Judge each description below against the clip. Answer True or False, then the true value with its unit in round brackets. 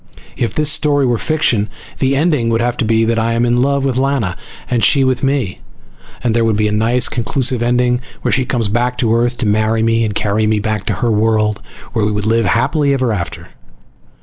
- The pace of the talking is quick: True (225 wpm)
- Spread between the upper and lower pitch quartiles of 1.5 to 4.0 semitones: True (3.0 semitones)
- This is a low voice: True (115 Hz)